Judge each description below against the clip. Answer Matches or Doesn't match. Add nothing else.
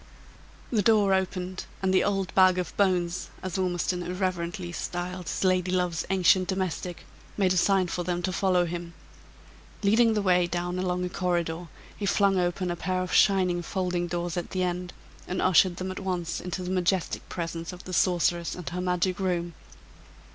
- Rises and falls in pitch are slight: Matches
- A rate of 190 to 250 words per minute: Doesn't match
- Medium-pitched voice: Matches